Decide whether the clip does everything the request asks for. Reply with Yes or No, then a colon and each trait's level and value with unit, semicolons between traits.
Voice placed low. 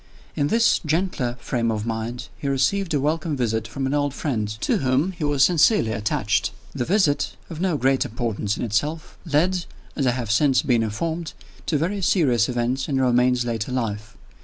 Yes: low, 130 Hz